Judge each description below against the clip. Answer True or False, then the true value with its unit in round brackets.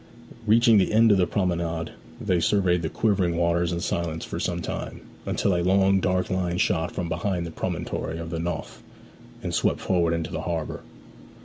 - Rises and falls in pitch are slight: True (2.2 semitones)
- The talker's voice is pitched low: True (85 Hz)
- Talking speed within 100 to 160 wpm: False (185 wpm)